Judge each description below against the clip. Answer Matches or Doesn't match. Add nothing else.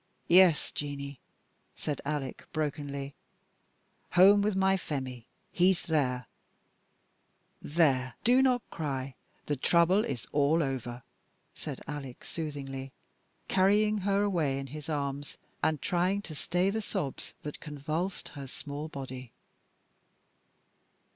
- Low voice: Doesn't match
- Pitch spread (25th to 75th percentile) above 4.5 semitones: Matches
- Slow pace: Matches